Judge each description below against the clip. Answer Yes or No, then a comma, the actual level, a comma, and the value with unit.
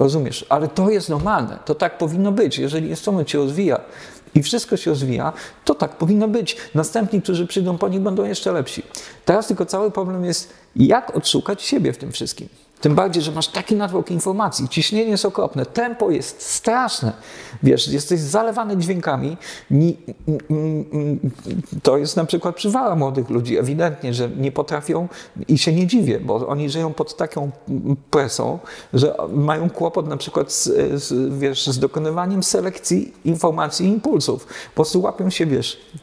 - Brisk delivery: Yes, fast, 170 wpm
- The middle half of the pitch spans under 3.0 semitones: No, average, 4.6 semitones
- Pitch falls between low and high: Yes, medium, 165 Hz